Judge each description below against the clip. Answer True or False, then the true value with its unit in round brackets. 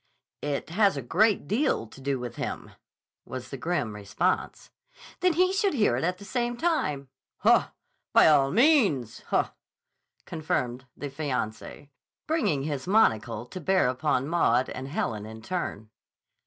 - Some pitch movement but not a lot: False (8.2 semitones)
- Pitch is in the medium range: True (145 Hz)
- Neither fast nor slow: True (150 wpm)